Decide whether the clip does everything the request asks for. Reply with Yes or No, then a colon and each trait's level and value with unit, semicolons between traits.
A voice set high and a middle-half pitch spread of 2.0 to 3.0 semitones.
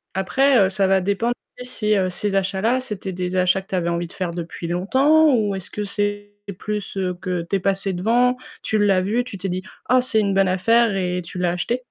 No: high, 195 Hz; average, 3.4 semitones